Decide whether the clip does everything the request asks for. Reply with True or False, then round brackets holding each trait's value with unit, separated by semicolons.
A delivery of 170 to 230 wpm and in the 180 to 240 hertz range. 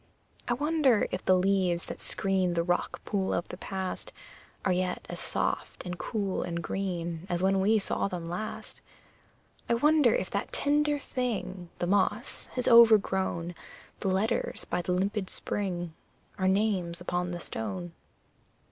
False (155 wpm; 190 Hz)